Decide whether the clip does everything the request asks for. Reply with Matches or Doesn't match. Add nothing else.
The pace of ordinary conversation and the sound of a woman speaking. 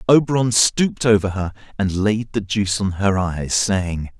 Doesn't match